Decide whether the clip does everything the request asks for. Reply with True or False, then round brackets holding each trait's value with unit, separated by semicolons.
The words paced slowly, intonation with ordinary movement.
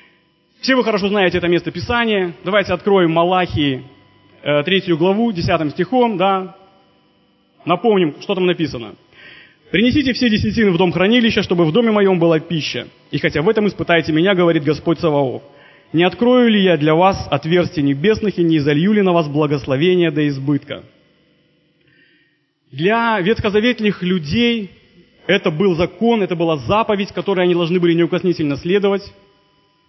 False (145 wpm; 4.1 semitones)